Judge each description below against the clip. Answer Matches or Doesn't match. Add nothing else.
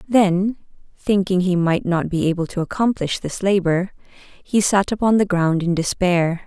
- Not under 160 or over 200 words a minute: Matches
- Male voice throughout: Doesn't match